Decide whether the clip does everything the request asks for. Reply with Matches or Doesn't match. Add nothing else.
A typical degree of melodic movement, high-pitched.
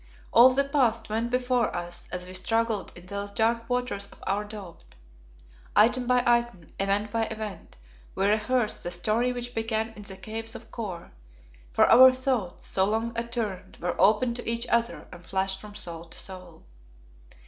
Matches